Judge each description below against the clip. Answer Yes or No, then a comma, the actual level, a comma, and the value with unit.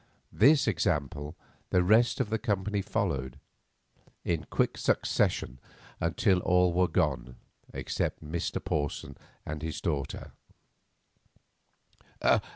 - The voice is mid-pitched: No, very low, 85 Hz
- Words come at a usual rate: No, slow, 100 wpm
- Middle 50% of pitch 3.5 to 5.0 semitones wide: Yes, average, 4.7 semitones